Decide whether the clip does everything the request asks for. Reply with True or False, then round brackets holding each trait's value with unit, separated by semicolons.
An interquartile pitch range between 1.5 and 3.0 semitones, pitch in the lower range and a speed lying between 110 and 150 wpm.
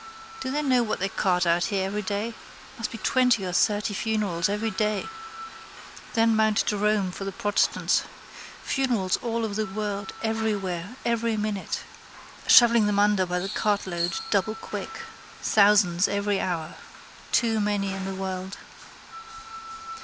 False (2.5 semitones; 205 Hz; 140 wpm)